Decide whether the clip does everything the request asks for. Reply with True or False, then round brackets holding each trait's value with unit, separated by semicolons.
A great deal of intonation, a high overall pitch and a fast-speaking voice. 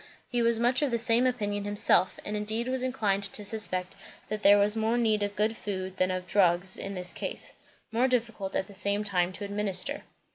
False (2.9 semitones; 210 Hz; 210 wpm)